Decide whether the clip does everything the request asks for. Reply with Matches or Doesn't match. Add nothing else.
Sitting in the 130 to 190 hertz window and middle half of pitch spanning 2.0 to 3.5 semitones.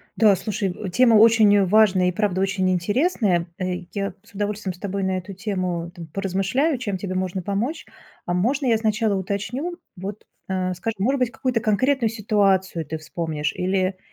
Doesn't match